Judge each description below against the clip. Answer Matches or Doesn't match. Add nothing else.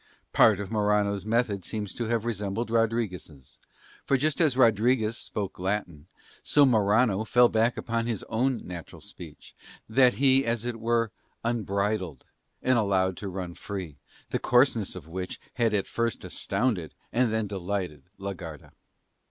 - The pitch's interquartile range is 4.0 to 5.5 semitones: Doesn't match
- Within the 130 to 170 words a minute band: Matches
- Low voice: Matches